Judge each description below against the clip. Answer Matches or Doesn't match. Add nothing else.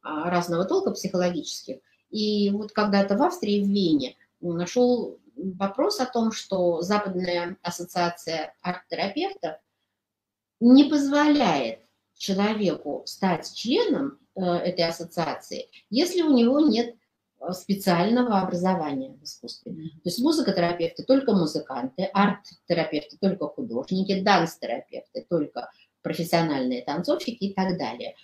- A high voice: Matches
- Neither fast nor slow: Doesn't match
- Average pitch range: Doesn't match